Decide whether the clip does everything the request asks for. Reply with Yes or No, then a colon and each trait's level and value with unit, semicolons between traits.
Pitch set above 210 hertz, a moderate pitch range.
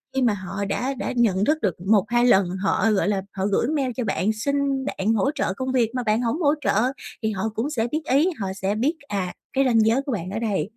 Yes: high, 225 Hz; average, 4.8 semitones